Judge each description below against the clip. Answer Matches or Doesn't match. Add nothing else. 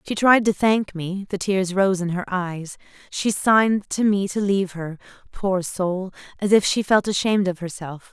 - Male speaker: Doesn't match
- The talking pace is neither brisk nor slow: Matches